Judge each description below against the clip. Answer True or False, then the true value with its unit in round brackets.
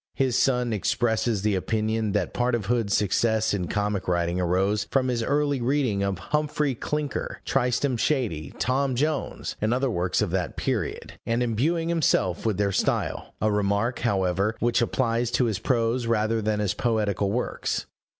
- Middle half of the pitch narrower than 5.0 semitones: True (3.7 semitones)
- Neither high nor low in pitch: False (115 Hz)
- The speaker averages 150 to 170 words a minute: True (165 wpm)